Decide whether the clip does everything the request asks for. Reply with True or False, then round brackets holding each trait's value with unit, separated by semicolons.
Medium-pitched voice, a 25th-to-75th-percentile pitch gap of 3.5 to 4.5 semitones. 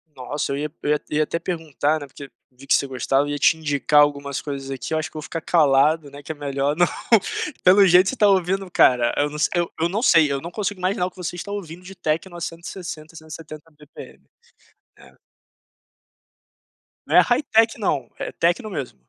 True (155 Hz; 3.8 semitones)